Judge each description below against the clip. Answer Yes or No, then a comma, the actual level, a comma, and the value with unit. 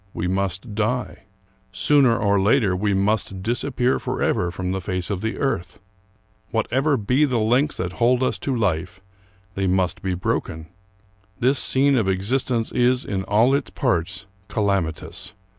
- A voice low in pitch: Yes, low, 105 Hz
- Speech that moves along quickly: No, average, 155 wpm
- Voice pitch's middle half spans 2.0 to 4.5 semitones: No, average, 4.9 semitones